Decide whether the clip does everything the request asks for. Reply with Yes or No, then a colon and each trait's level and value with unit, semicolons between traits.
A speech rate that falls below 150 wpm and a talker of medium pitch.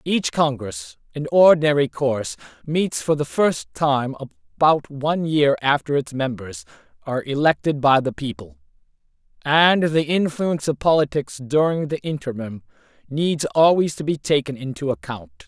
Yes: average, 140 wpm; medium, 145 Hz